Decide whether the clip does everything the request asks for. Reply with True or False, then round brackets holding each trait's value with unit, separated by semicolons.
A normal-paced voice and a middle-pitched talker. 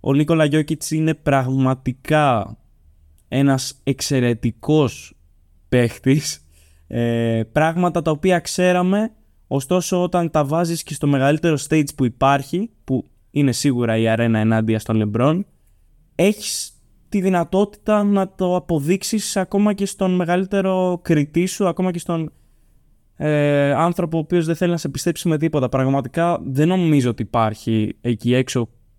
True (130 wpm; 150 Hz)